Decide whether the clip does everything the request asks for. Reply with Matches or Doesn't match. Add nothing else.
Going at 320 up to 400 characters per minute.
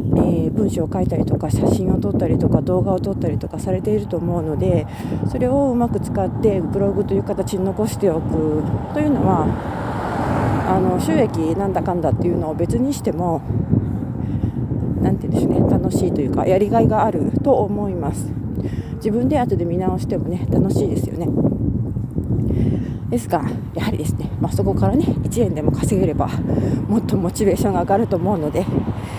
Matches